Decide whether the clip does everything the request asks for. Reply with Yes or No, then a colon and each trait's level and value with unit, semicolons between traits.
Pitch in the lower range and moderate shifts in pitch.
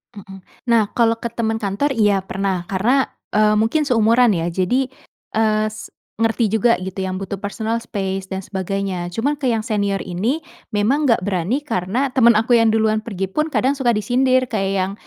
No: high, 215 Hz; average, 3.6 semitones